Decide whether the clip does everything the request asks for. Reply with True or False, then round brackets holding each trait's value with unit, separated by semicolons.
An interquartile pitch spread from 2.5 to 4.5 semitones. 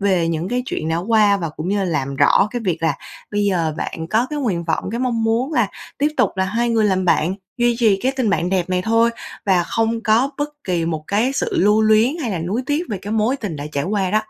False (4.9 semitones)